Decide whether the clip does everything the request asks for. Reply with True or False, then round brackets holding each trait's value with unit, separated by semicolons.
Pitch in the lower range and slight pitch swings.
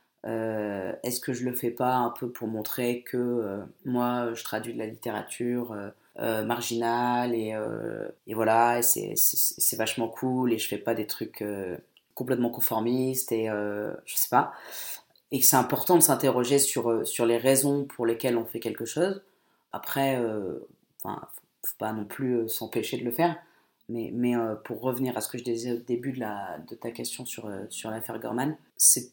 True (120 Hz; 2.3 semitones)